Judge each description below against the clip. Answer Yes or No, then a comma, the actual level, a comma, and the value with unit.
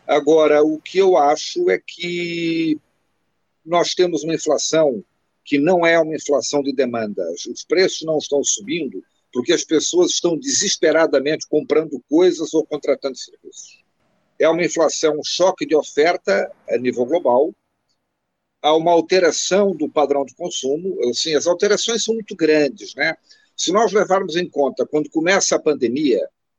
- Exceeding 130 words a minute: Yes, average, 150 wpm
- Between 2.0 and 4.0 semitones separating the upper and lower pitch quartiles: No, average, 4.8 semitones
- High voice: No, medium, 165 Hz